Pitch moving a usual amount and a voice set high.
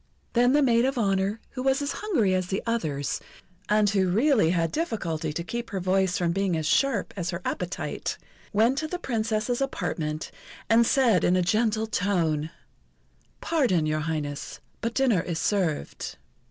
No: wide, 5.8 semitones; high, 200 Hz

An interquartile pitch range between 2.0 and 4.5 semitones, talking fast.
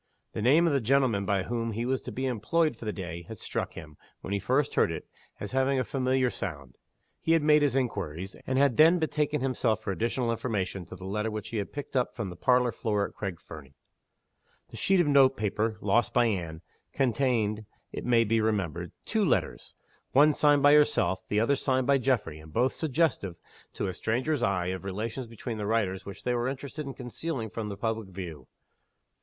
No: average, 5.2 semitones; fast, 210 wpm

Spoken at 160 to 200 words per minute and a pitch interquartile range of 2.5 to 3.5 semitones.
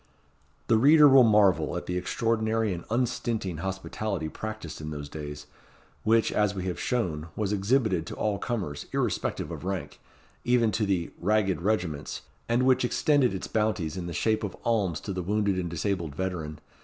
No: average, 170 wpm; average, 4.5 semitones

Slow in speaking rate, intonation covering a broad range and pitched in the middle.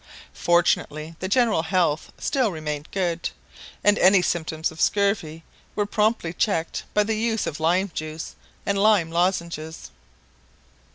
No: slow, 130 wpm; average, 4.1 semitones; medium, 175 Hz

